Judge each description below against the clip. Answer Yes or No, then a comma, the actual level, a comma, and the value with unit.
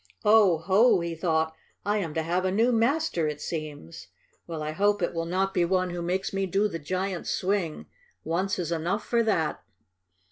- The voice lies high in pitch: No, medium, 180 Hz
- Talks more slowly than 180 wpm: No, average, 190 wpm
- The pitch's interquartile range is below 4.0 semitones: Yes, average, 3.3 semitones